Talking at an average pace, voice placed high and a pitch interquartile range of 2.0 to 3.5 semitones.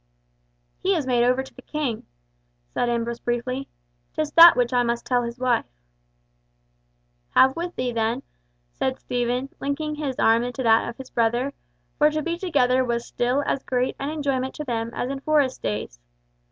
Yes: average, 175 wpm; very high, 255 Hz; average, 2.9 semitones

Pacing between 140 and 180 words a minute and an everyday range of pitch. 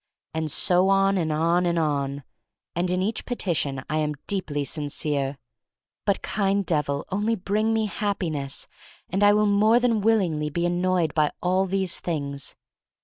Yes: average, 160 wpm; average, 4.8 semitones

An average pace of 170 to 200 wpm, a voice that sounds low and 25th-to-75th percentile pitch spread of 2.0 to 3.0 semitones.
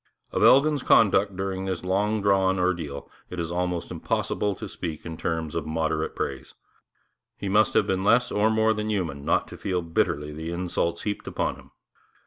No: average, 180 wpm; very low, 95 Hz; average, 3.7 semitones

